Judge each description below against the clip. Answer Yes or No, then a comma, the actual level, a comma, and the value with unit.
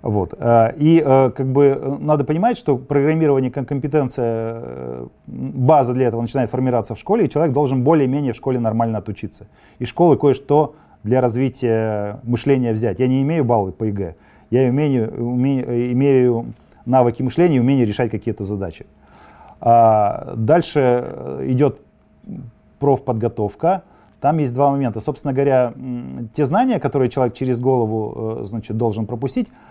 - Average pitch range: Yes, average, 3.5 semitones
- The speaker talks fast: No, average, 135 wpm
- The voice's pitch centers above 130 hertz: No, low, 125 Hz